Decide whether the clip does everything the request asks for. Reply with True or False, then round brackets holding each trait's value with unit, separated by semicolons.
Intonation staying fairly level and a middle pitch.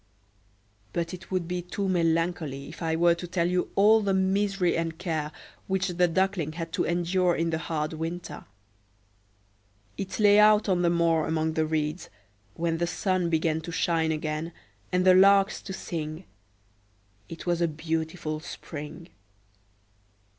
True (2.3 semitones; 170 Hz)